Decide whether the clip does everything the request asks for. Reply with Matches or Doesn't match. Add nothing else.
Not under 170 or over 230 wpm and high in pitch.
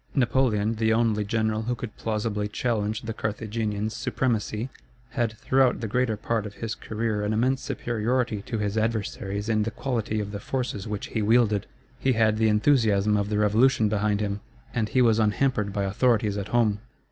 Doesn't match